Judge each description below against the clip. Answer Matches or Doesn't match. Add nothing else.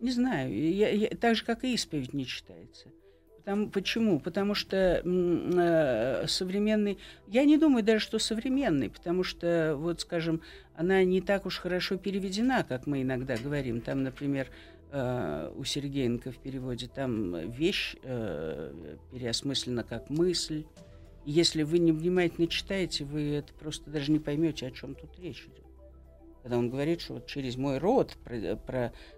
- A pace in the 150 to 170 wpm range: Matches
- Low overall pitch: Doesn't match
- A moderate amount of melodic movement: Doesn't match